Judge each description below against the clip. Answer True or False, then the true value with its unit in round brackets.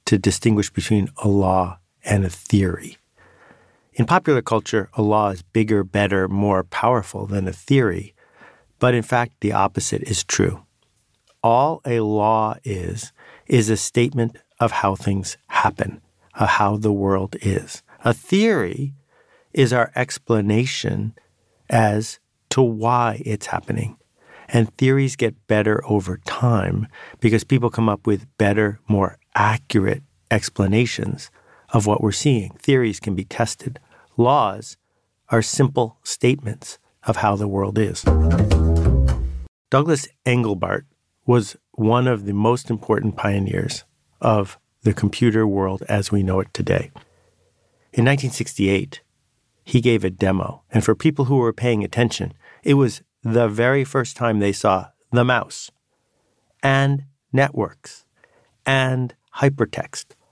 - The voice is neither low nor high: False (110 Hz)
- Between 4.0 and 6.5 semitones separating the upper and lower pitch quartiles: False (3.5 semitones)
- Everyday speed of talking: False (130 wpm)